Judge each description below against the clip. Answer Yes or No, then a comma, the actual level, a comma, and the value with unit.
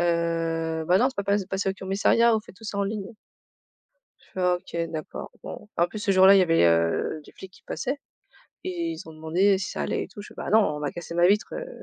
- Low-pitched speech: No, high, 190 Hz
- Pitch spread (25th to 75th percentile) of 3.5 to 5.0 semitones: Yes, average, 3.8 semitones